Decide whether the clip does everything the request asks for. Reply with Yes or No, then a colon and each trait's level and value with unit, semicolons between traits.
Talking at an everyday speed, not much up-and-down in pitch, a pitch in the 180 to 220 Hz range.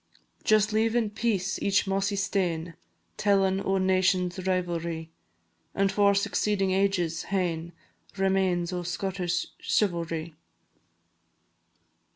No: slow, 100 wpm; narrow, 2.2 semitones; high, 190 Hz